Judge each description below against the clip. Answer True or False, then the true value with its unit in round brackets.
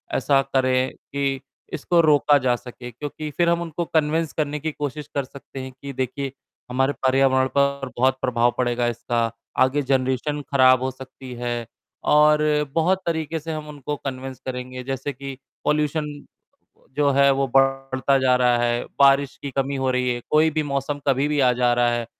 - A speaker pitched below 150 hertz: True (135 Hz)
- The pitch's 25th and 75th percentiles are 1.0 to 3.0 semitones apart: True (2.4 semitones)